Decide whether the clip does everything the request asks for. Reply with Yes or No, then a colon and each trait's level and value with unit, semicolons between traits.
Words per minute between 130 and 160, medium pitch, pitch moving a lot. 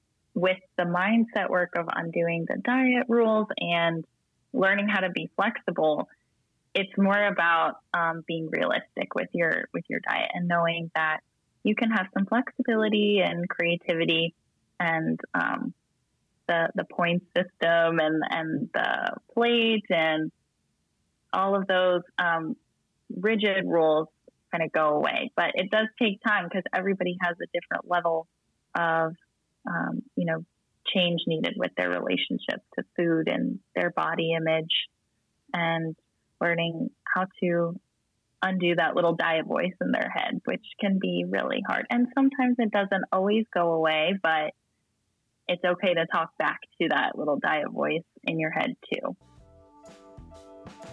No: average, 145 wpm; medium, 175 Hz; average, 3.5 semitones